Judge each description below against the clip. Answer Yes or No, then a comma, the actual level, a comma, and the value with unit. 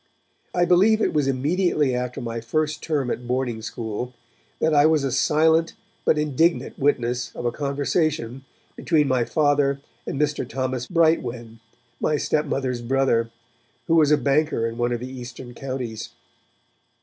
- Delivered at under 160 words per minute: Yes, average, 150 wpm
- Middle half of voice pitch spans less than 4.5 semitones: Yes, average, 3.9 semitones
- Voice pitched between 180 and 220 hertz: No, low, 135 Hz